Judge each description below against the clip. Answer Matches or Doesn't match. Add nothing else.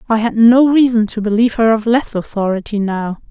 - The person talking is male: Doesn't match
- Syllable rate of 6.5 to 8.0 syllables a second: Doesn't match